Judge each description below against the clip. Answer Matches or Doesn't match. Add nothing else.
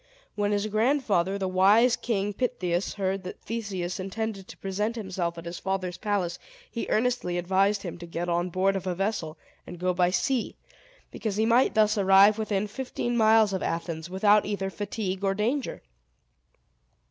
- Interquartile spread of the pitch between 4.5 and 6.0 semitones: Doesn't match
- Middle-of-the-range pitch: Doesn't match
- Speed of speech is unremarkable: Matches